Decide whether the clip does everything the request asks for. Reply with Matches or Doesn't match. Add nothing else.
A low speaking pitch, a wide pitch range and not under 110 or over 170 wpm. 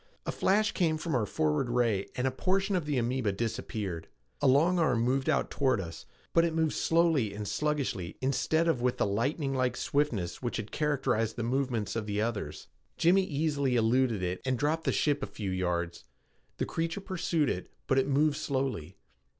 Doesn't match